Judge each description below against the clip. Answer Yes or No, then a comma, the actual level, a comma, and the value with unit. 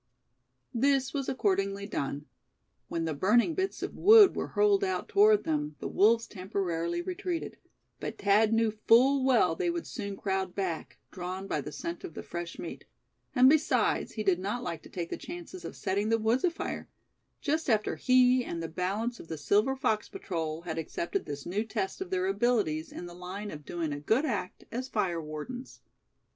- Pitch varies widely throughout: Yes, wide, 7.0 semitones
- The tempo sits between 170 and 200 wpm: Yes, average, 185 wpm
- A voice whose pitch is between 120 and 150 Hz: No, high, 210 Hz